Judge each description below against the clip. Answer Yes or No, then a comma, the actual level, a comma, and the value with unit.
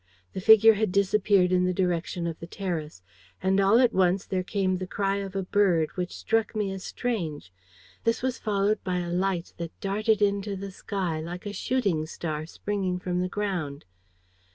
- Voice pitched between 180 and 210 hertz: Yes, high, 190 Hz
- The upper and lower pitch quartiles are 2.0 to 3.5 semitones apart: Yes, narrow, 2.5 semitones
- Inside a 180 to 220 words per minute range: Yes, average, 185 wpm